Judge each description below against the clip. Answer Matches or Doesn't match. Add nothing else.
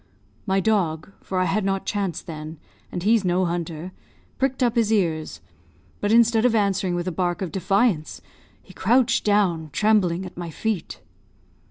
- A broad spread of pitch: Doesn't match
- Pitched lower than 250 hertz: Matches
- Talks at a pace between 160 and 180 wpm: Matches